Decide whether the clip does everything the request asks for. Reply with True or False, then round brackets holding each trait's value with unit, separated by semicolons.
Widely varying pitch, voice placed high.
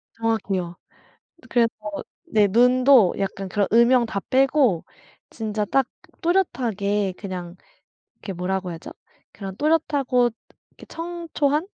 True (5.7 semitones; 225 Hz)